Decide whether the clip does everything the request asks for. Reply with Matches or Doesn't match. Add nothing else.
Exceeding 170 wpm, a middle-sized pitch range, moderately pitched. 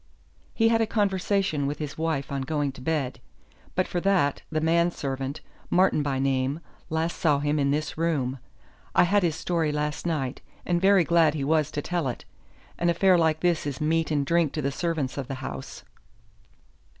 Matches